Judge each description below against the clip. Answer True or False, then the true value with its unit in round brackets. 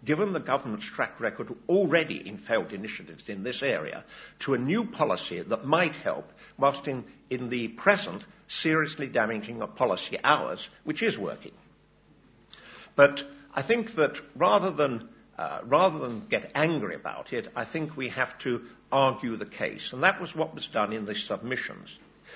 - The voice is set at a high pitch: False (135 Hz)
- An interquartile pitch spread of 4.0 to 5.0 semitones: True (4.7 semitones)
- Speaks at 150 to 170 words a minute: True (165 wpm)